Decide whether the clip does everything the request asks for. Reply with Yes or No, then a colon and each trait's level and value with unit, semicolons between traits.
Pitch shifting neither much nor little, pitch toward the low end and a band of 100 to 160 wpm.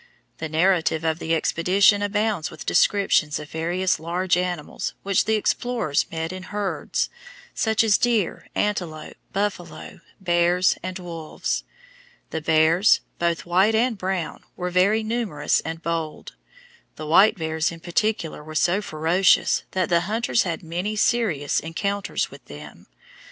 No: average, 4.0 semitones; medium, 180 Hz; average, 140 wpm